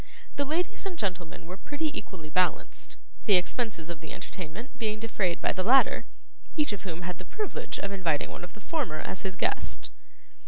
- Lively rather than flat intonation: Yes, wide, 6.1 semitones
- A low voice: No, high, 195 Hz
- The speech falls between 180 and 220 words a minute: Yes, average, 190 wpm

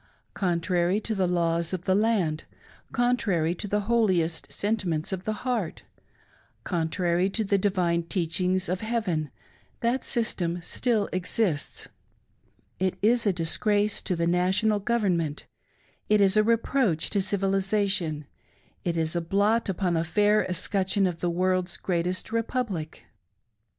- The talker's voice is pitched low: No, medium, 185 Hz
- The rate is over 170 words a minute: No, slow, 135 wpm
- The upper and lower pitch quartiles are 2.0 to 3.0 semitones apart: No, average, 3.7 semitones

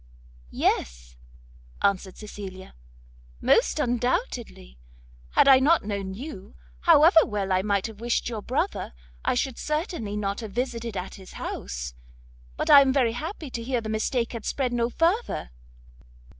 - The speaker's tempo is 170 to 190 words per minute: No, average, 145 wpm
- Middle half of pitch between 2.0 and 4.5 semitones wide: No, average, 5.1 semitones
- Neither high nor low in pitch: No, high, 230 Hz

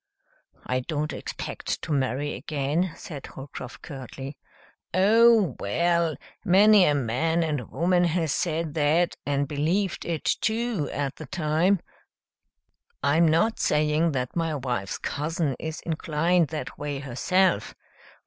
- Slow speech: Yes, slow, 125 wpm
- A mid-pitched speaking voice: Yes, medium, 155 Hz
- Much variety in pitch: No, average, 3.5 semitones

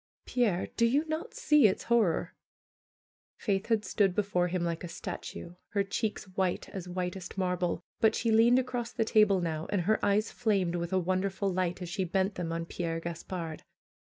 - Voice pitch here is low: No, high, 190 Hz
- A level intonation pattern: No, average, 3.5 semitones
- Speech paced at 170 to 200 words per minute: Yes, average, 180 wpm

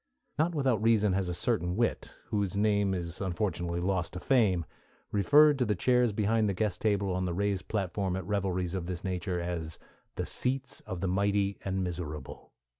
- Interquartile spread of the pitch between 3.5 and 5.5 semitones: No, average, 3.1 semitones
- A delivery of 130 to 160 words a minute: No, average, 185 wpm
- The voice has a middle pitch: No, very low, 95 Hz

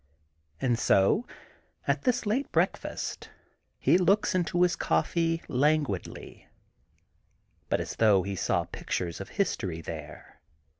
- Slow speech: Yes, slow, 115 wpm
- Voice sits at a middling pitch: Yes, medium, 150 Hz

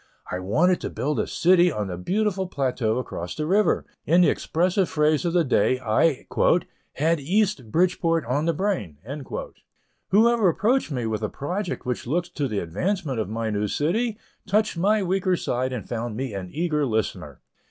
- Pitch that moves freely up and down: Yes, wide, 7.6 semitones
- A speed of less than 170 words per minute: No, average, 175 wpm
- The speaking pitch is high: No, medium, 155 Hz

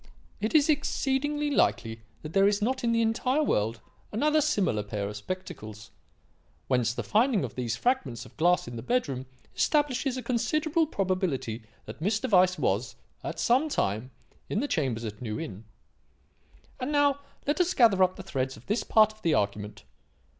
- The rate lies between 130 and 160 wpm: No, average, 175 wpm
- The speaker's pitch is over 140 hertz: Yes, high, 190 Hz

